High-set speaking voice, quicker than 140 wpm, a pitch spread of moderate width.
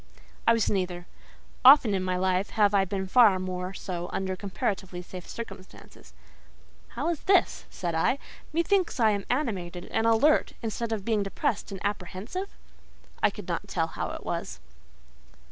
Yes: high, 195 Hz; average, 160 wpm; average, 3.9 semitones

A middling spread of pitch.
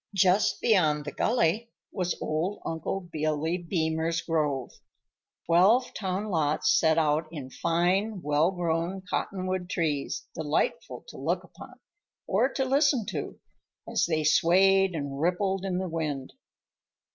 Yes: average, 3.5 semitones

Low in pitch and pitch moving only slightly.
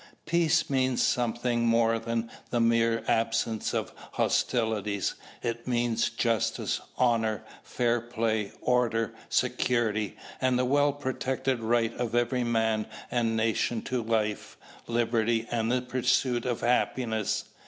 Yes: low, 115 Hz; narrow, 1.7 semitones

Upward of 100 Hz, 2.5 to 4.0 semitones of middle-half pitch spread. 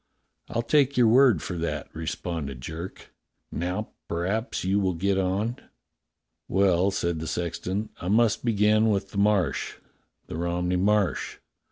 No: very low, 95 Hz; average, 3.6 semitones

